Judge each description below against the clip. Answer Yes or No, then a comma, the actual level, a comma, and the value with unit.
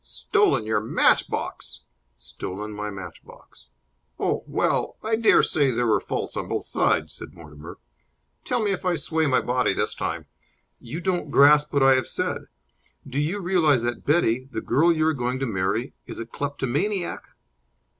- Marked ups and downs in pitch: Yes, wide, 6.2 semitones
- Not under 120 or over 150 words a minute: No, average, 165 wpm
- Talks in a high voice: No, low, 135 Hz